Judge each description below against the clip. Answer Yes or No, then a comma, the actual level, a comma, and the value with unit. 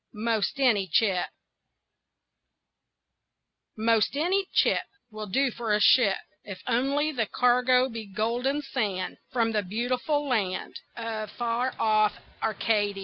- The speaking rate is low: Yes, slow, 120 wpm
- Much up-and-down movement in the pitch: No, average, 3.2 semitones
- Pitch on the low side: No, high, 230 Hz